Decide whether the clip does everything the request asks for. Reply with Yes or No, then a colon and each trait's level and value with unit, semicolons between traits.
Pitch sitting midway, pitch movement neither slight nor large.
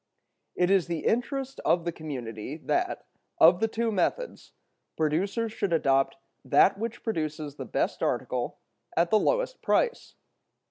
No: medium, 180 Hz; wide, 6.9 semitones